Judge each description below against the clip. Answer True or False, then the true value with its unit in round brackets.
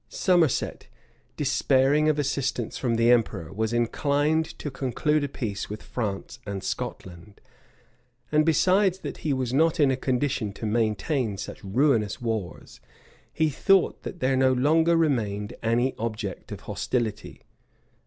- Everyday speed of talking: True (145 wpm)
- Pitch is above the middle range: False (130 Hz)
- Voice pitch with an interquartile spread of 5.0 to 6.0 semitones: True (5.3 semitones)